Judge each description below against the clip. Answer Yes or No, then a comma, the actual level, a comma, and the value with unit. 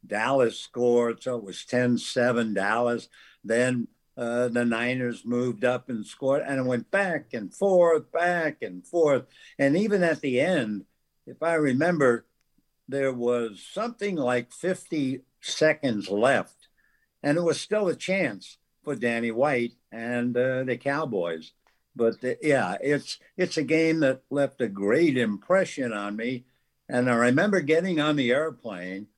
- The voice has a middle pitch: No, low, 125 Hz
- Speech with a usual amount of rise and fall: Yes, average, 4.7 semitones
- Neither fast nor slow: Yes, average, 150 wpm